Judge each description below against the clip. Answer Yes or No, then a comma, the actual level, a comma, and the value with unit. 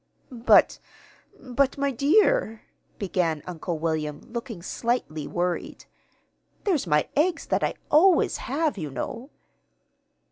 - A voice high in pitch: Yes, high, 230 Hz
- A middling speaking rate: No, slow, 110 wpm